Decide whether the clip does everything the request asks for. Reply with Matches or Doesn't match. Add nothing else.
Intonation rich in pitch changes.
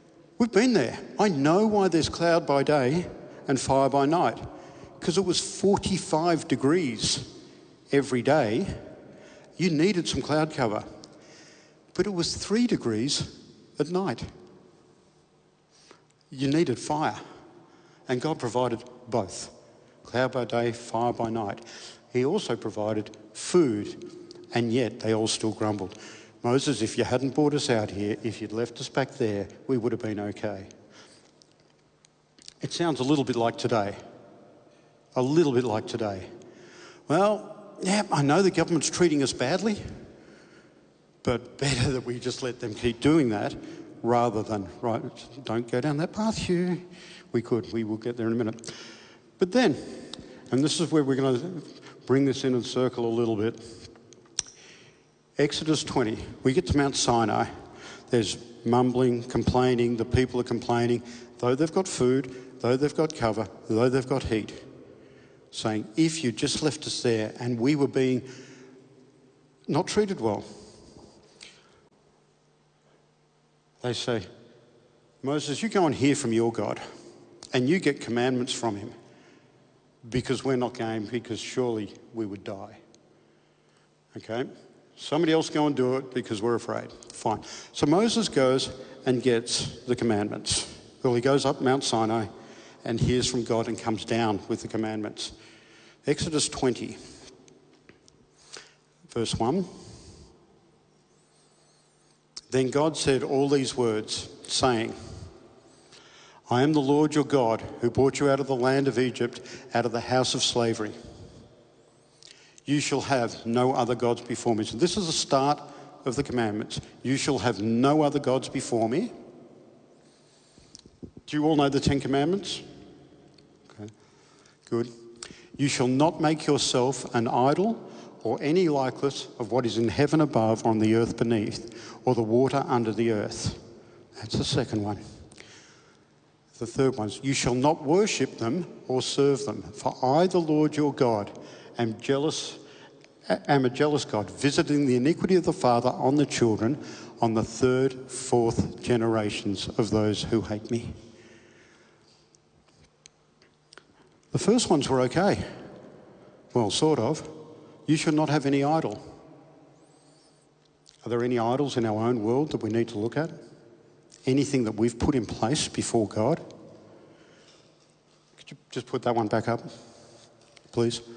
Doesn't match